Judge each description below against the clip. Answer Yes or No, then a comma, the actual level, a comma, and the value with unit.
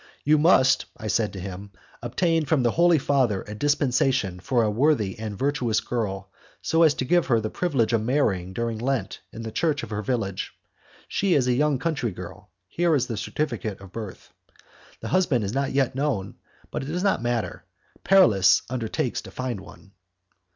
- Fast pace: No, average, 185 wpm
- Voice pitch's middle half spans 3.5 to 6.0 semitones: Yes, wide, 5.5 semitones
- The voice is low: Yes, low, 120 Hz